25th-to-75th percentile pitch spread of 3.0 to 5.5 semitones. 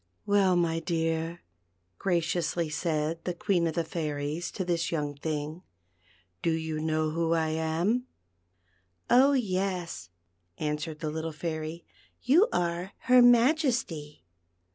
No: narrow, 2.6 semitones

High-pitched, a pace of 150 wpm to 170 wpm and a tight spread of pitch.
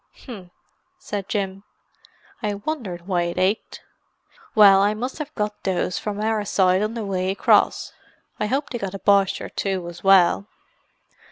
Yes: high, 200 Hz; average, 165 wpm; narrow, 2.2 semitones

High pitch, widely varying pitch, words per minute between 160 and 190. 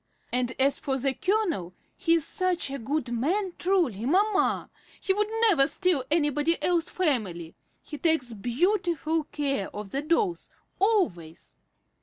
No: very high, 305 Hz; wide, 6.4 semitones; average, 145 wpm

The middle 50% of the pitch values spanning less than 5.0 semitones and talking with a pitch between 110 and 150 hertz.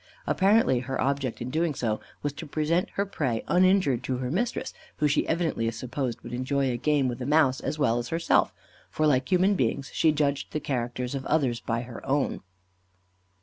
Yes: average, 3.8 semitones; medium, 140 Hz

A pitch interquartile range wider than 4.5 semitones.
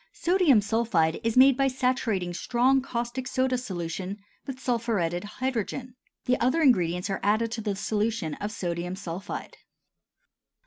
Yes: average, 5.2 semitones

